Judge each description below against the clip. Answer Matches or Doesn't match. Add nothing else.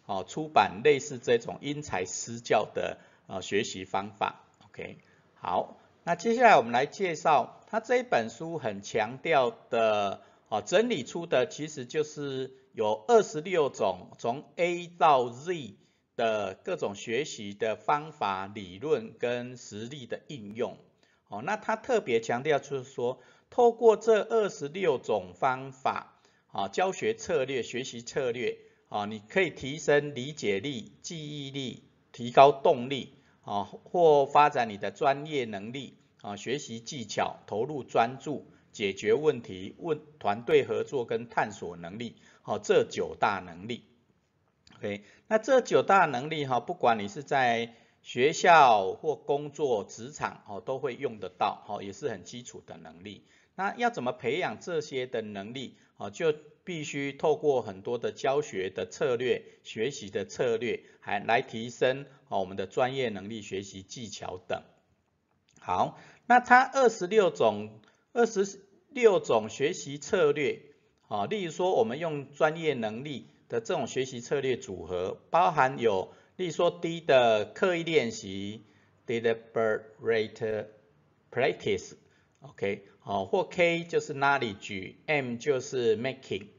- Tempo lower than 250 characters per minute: Matches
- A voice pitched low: Doesn't match